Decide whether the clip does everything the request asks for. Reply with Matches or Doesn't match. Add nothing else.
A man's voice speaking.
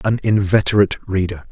Matches